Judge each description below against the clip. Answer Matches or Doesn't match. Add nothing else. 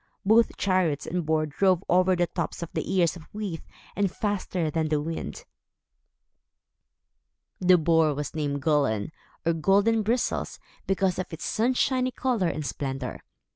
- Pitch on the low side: Doesn't match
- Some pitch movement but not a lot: Matches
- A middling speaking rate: Matches